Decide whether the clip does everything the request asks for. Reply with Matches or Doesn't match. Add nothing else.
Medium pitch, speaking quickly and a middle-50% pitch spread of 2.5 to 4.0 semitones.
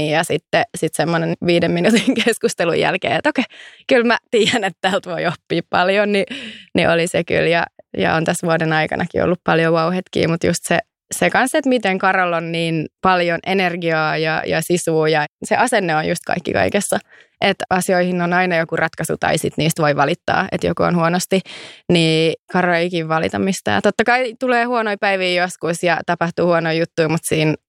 Matches